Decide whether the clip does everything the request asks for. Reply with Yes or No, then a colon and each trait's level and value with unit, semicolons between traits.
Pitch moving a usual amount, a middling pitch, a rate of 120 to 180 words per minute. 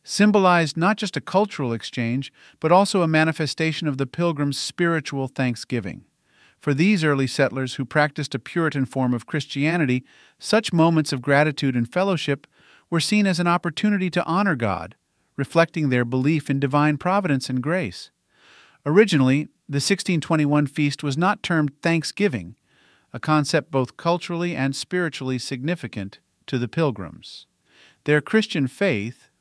Yes: average, 4.3 semitones; medium, 150 Hz; average, 140 wpm